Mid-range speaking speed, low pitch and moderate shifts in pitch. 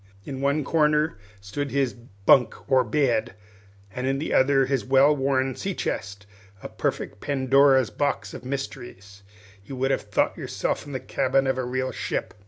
No: average, 170 wpm; low, 130 Hz; narrow, 2.0 semitones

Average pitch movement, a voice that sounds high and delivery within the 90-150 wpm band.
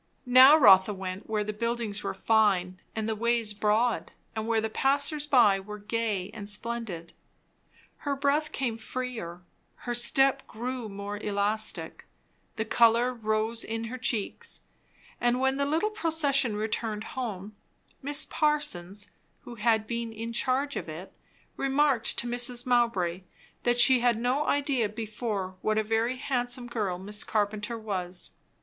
Yes: average, 3.3 semitones; high, 230 Hz; average, 145 wpm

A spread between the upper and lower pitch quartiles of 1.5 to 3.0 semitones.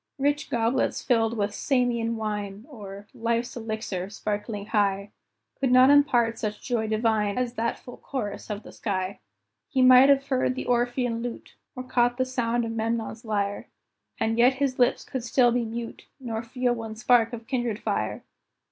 Yes: narrow, 2.4 semitones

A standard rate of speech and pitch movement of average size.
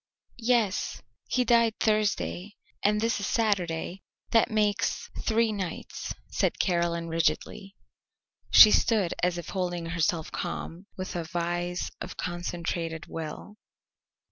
No: slow, 115 wpm; average, 3.8 semitones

